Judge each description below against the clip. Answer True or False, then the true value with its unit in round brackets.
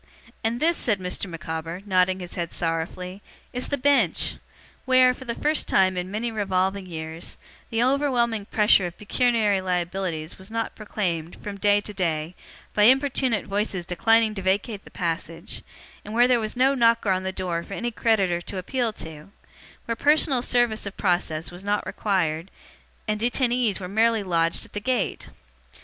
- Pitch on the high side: True (205 Hz)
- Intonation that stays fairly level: False (4.4 semitones)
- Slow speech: False (165 wpm)